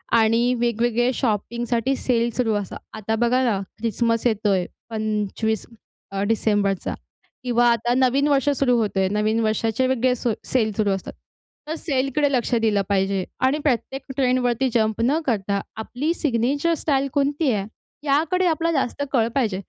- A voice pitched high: Yes, high, 235 Hz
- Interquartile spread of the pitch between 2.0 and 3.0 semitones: No, average, 3.6 semitones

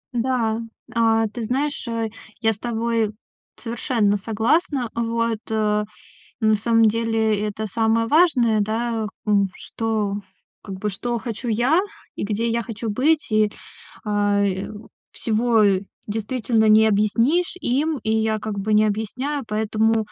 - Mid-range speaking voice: No, high, 225 Hz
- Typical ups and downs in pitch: No, narrow, 1.7 semitones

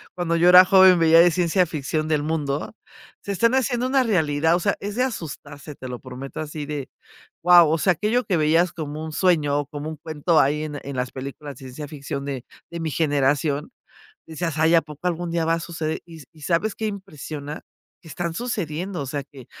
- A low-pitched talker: No, medium, 160 Hz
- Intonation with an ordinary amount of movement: Yes, average, 3.4 semitones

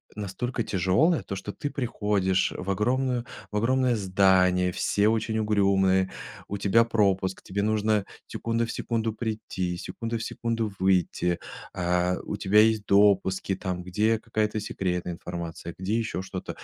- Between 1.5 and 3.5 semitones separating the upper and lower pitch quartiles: Yes, average, 3.1 semitones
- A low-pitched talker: Yes, low, 100 Hz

